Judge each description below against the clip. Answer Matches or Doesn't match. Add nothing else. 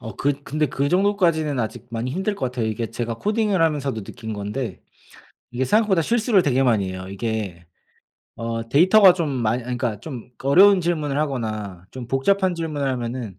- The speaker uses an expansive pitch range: Matches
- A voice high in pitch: Doesn't match